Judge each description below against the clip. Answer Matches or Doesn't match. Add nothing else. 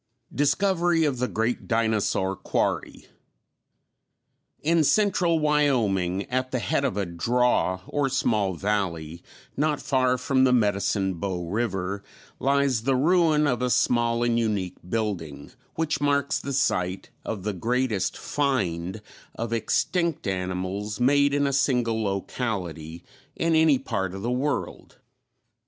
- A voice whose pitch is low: Matches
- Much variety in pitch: Matches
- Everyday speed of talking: Doesn't match